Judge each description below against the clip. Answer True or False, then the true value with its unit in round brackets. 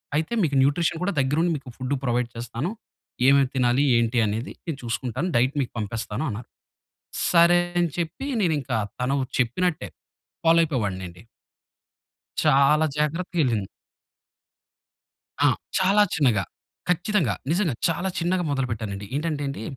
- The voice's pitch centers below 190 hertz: True (140 Hz)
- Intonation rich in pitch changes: True (5.8 semitones)